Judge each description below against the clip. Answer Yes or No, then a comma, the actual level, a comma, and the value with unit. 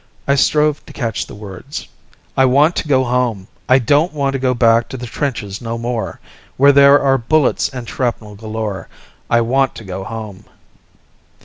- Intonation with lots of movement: No, average, 3.6 semitones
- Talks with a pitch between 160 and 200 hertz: No, low, 125 Hz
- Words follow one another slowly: No, average, 180 wpm